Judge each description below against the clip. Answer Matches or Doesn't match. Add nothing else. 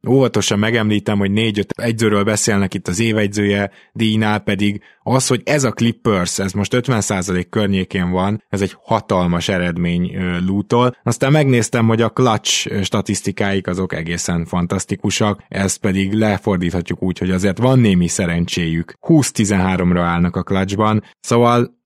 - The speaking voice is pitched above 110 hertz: Doesn't match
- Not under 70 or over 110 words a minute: Doesn't match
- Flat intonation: Doesn't match